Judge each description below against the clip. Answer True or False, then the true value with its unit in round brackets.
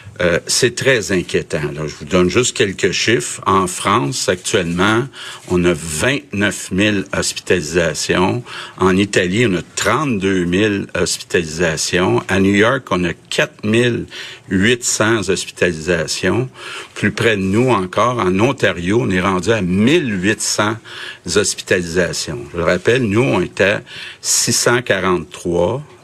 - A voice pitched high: False (95 Hz)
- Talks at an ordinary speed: False (125 wpm)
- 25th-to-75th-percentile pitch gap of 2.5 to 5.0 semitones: True (4.5 semitones)